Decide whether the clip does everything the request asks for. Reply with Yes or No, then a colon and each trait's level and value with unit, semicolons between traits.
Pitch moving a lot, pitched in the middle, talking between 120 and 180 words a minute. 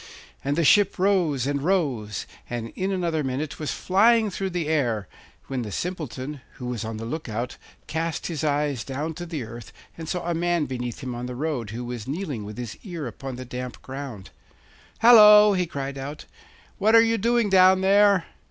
No: wide, 6.7 semitones; medium, 150 Hz; average, 195 wpm